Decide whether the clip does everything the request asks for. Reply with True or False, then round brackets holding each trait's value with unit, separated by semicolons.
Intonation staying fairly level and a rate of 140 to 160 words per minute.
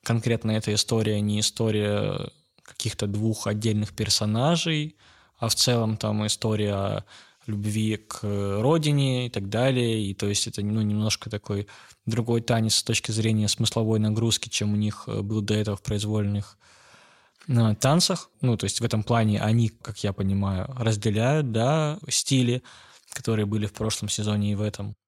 True (2.0 semitones; 155 wpm)